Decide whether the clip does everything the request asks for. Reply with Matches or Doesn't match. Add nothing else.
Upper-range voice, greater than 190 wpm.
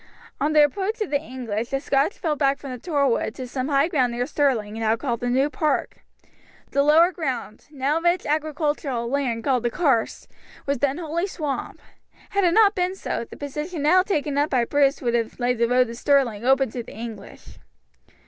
Matches